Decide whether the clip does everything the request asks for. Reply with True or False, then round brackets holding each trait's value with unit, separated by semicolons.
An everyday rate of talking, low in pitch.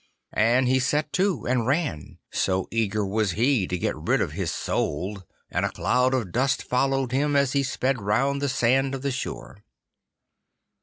True (175 wpm; 130 Hz)